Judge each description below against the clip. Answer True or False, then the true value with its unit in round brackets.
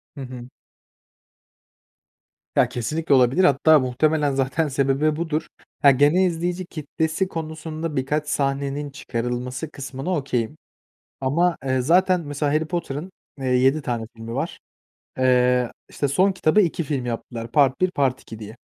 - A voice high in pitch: False (145 Hz)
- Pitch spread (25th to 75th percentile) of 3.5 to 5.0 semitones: True (3.8 semitones)